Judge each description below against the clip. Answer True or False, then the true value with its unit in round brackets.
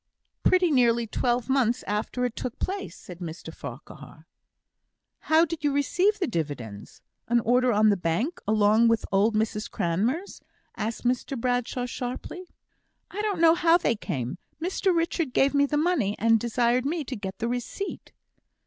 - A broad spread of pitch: True (6.7 semitones)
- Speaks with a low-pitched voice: False (245 Hz)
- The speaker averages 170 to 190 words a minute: False (160 wpm)